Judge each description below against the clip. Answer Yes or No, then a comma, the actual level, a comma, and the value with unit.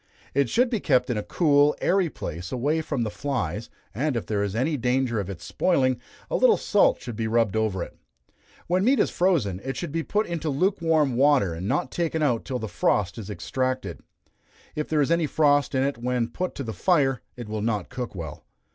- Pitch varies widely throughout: Yes, wide, 6.1 semitones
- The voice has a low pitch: Yes, low, 130 Hz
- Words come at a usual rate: No, fast, 215 wpm